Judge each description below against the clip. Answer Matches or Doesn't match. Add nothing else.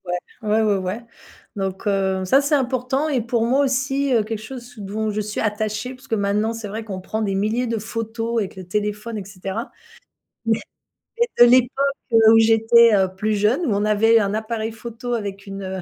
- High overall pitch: Matches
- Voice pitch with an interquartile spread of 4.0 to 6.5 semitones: Doesn't match